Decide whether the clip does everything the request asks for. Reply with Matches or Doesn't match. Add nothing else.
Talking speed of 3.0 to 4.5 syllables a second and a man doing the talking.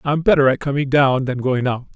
Doesn't match